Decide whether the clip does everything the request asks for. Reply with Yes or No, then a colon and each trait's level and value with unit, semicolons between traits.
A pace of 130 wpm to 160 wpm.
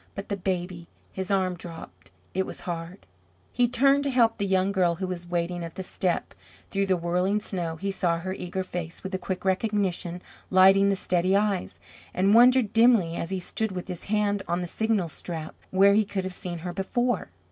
No: average, 200 wpm